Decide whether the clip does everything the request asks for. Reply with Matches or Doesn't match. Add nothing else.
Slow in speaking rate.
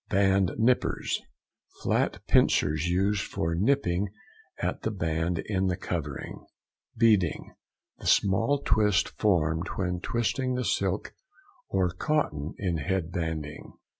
Matches